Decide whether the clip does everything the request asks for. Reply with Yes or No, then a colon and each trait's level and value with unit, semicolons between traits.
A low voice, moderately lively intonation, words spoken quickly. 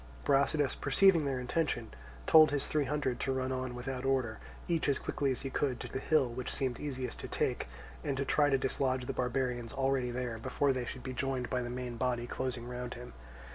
No: low, 130 Hz; narrow, 1.9 semitones; fast, 215 wpm